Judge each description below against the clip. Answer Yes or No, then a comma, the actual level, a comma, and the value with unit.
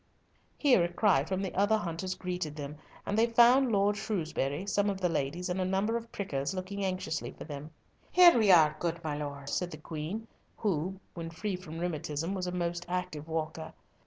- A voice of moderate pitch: Yes, medium, 180 Hz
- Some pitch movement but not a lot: Yes, average, 4.0 semitones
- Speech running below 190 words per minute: No, average, 195 wpm